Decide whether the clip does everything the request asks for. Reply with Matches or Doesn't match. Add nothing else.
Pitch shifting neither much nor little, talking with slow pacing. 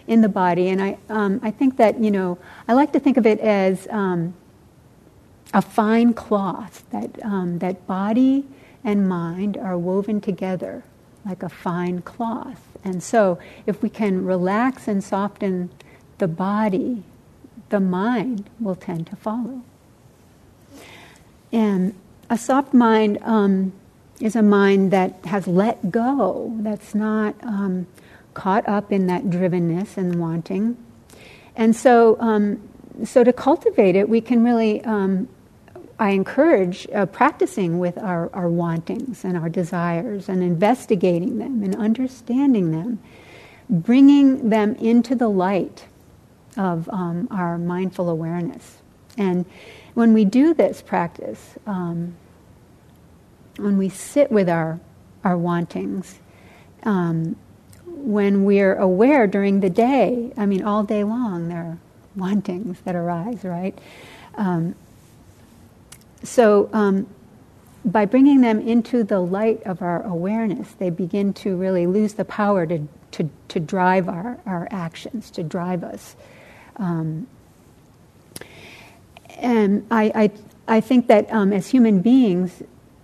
Matches